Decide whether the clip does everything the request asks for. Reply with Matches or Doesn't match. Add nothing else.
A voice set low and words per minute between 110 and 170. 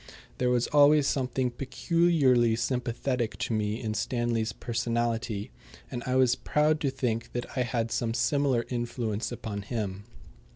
Matches